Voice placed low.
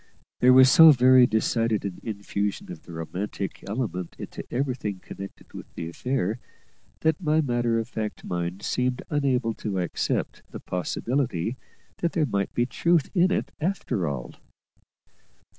Yes: low, 115 Hz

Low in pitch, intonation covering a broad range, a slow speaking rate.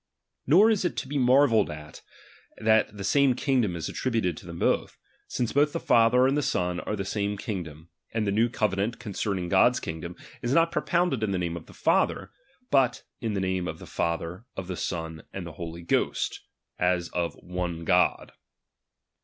No: low, 100 Hz; wide, 5.9 semitones; fast, 205 wpm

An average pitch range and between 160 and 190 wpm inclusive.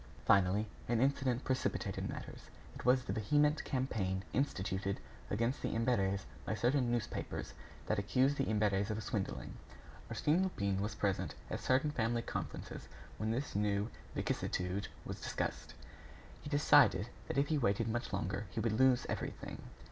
No: average, 4.6 semitones; average, 150 wpm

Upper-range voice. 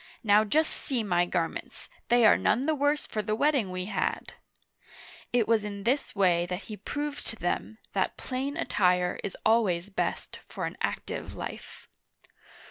Yes: high, 215 Hz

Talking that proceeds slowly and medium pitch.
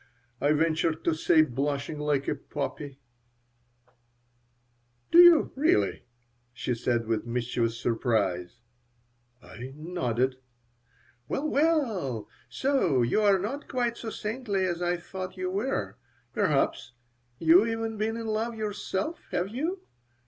Yes: slow, 125 wpm; medium, 175 Hz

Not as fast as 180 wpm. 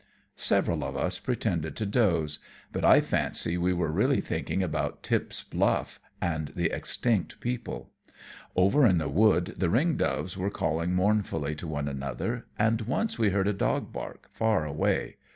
Yes: average, 165 wpm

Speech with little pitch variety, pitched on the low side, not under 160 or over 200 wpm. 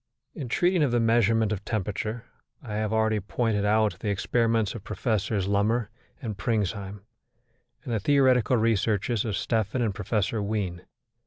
No: narrow, 2.3 semitones; low, 110 Hz; average, 150 wpm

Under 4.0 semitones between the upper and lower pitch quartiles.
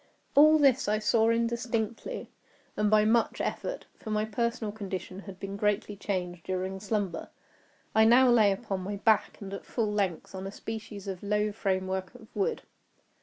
Yes: average, 2.8 semitones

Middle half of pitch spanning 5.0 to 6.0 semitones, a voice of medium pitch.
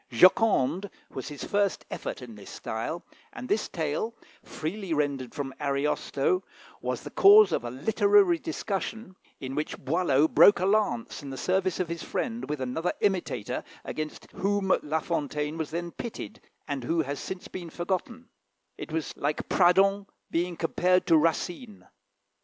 Yes: average, 5.3 semitones; medium, 170 Hz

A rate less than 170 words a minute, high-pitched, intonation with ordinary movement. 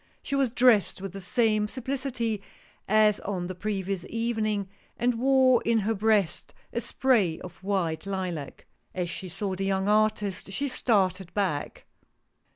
Yes: average, 150 wpm; high, 205 Hz; average, 3.4 semitones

